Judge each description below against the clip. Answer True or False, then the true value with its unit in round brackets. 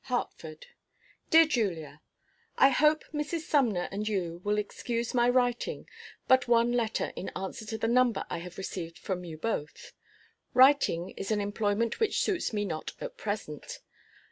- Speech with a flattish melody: False (5.2 semitones)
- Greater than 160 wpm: False (155 wpm)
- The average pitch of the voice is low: False (220 Hz)